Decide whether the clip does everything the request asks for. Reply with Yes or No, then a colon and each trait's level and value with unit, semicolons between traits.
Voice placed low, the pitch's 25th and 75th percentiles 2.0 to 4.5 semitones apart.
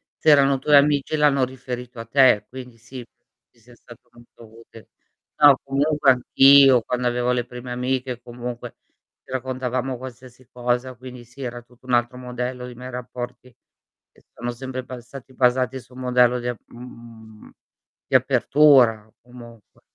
No: low, 125 Hz; narrow, 1.4 semitones